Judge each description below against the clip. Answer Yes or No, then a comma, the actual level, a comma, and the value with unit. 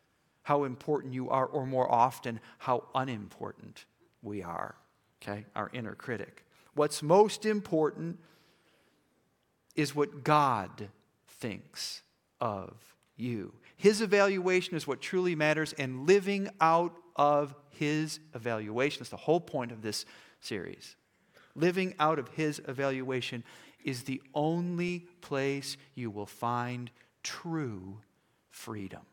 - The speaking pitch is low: No, medium, 145 Hz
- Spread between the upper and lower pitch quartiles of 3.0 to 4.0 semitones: No, average, 5.1 semitones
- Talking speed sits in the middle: No, slow, 115 wpm